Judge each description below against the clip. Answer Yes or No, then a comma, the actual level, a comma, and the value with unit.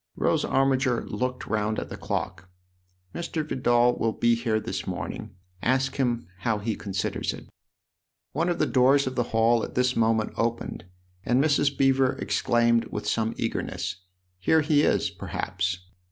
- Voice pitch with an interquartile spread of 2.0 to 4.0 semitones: Yes, average, 3.4 semitones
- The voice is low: Yes, low, 120 Hz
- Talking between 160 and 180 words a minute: Yes, average, 165 wpm